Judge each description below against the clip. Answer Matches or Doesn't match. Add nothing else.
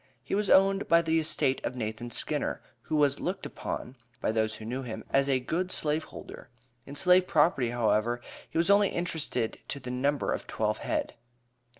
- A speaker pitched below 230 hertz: Matches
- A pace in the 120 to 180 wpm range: Doesn't match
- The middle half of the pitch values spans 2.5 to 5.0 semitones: Doesn't match